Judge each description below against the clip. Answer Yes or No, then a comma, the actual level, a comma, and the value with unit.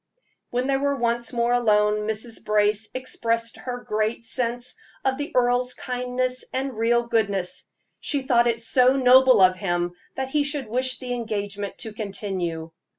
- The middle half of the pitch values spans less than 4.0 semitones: Yes, average, 3.2 semitones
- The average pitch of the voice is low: No, high, 235 Hz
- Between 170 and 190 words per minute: No, average, 155 wpm